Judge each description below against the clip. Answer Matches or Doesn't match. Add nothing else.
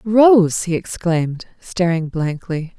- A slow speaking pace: Matches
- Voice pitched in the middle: Matches